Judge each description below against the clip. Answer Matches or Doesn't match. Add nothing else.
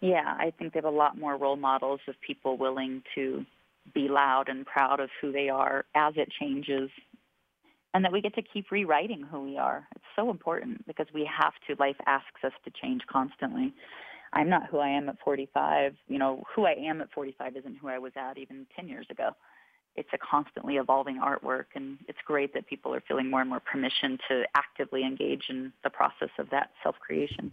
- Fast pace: Matches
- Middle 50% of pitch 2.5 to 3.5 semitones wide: Matches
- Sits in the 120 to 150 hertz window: Matches